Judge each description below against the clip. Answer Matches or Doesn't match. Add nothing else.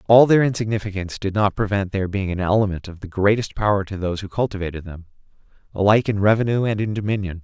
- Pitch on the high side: Doesn't match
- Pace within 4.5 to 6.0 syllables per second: Doesn't match